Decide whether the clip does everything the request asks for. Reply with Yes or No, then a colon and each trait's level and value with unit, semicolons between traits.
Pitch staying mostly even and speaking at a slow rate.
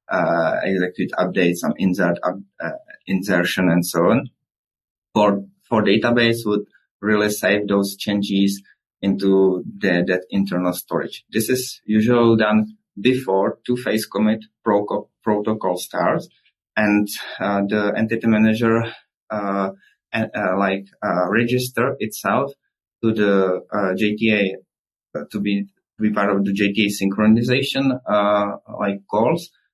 Yes: narrow, 1.9 semitones; slow, 125 wpm